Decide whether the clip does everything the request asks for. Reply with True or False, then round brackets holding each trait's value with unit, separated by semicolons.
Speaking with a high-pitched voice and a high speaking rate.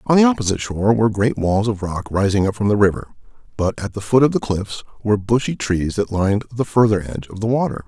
False (105 Hz; 245 wpm)